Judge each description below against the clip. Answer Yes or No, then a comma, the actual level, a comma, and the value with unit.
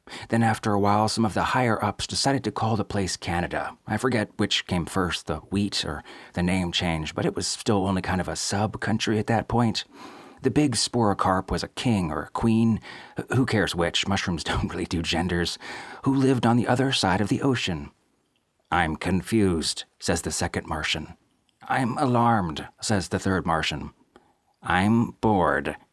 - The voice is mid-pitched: No, low, 100 Hz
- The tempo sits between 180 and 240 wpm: Yes, average, 185 wpm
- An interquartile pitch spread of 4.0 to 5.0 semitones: Yes, average, 4.4 semitones